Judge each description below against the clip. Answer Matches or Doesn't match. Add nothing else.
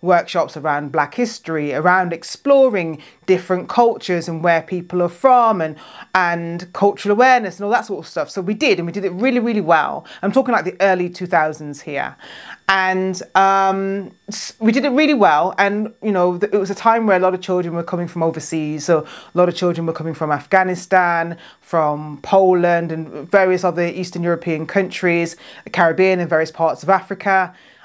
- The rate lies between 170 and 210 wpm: Matches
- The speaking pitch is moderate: Matches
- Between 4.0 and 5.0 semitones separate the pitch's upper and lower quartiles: Doesn't match